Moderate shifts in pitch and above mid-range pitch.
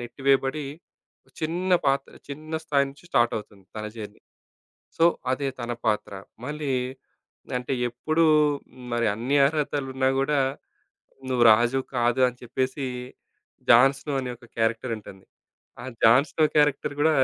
No: average, 3.5 semitones; low, 135 Hz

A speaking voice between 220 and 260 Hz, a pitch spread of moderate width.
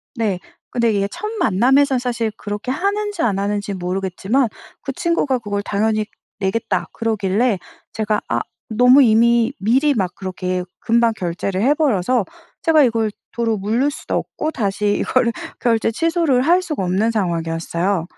Yes: high, 225 Hz; average, 4.6 semitones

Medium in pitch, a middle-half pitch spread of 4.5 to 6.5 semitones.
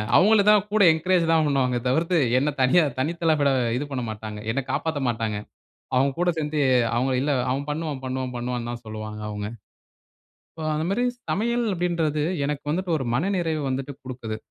Yes: medium, 145 Hz; average, 5.0 semitones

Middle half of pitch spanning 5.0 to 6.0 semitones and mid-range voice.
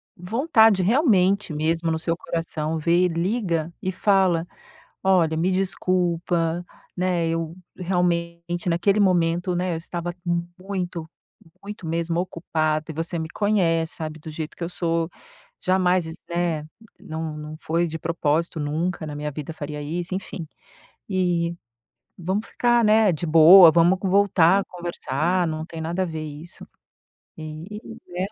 No: narrow, 2.4 semitones; medium, 170 Hz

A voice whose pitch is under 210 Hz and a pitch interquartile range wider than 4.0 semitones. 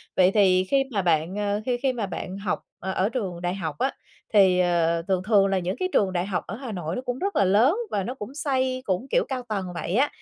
Yes: high, 200 Hz; wide, 5.4 semitones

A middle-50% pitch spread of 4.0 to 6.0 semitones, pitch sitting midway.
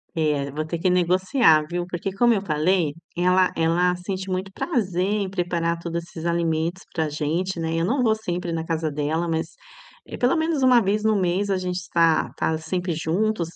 No: average, 2.8 semitones; medium, 175 Hz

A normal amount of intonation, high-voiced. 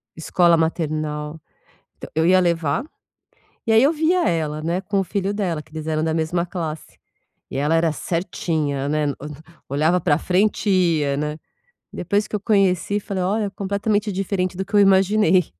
No: average, 4.1 semitones; medium, 175 Hz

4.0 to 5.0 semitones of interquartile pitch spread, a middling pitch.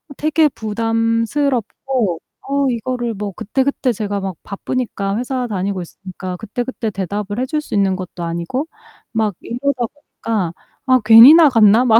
No: average, 4.4 semitones; high, 225 Hz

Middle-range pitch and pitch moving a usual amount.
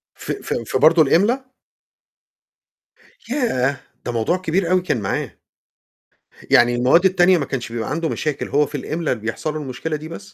No: medium, 155 Hz; wide, 5.8 semitones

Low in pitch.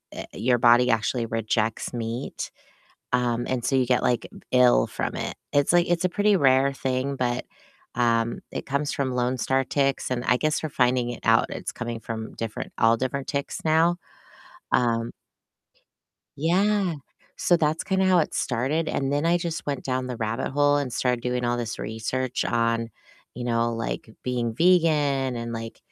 Yes: low, 125 Hz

